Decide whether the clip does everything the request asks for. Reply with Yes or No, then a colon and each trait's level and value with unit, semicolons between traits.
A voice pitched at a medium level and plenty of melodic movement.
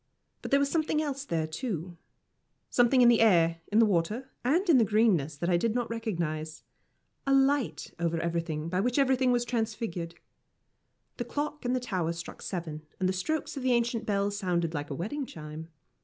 No: high, 215 Hz; wide, 7.1 semitones